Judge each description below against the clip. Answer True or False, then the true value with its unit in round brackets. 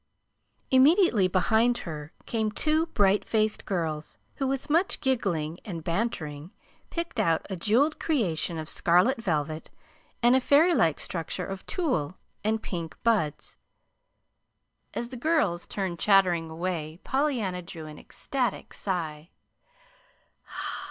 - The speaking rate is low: True (125 wpm)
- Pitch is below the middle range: False (195 Hz)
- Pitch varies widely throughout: True (7.3 semitones)